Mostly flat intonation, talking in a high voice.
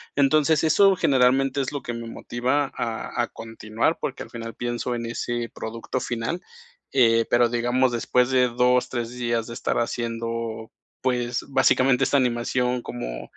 No: narrow, 1.9 semitones; low, 120 Hz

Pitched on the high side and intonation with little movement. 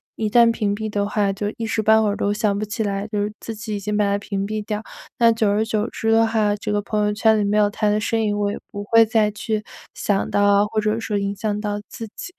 Yes: high, 210 Hz; narrow, 1.3 semitones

